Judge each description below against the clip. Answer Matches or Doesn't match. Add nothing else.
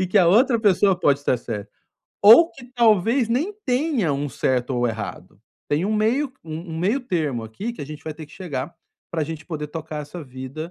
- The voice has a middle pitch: Matches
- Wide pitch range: Matches